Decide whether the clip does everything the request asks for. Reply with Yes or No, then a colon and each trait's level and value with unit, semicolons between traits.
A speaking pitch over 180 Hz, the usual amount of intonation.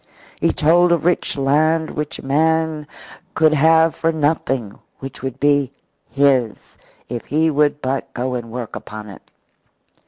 No: medium, 145 Hz; average, 3.4 semitones